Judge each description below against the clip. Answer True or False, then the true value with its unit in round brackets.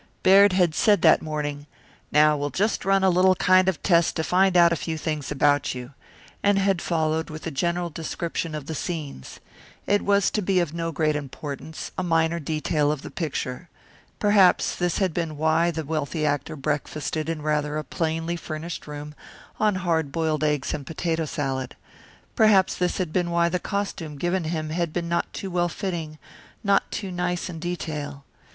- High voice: False (165 Hz)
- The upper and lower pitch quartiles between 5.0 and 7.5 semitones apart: False (2.8 semitones)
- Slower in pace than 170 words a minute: False (185 wpm)